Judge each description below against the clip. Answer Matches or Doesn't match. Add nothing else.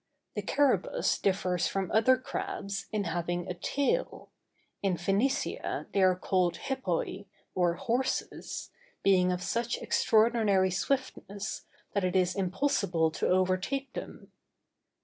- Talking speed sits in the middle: Doesn't match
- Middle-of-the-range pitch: Doesn't match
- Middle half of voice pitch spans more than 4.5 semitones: Matches